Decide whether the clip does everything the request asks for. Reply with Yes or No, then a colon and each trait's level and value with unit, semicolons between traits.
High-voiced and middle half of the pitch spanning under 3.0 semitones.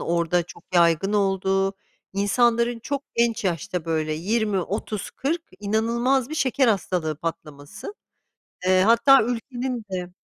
No: high, 200 Hz; average, 5.1 semitones